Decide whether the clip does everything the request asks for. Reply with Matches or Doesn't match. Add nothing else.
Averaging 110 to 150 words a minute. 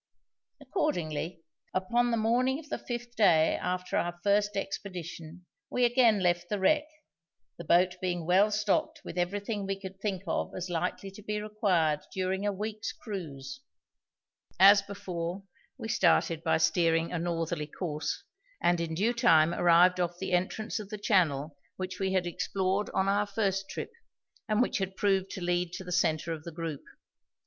Doesn't match